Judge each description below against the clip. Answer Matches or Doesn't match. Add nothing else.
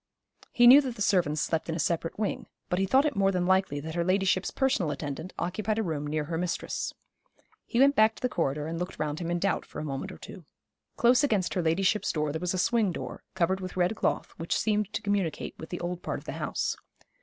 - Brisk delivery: Matches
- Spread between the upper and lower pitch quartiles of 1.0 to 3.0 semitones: Doesn't match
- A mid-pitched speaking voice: Matches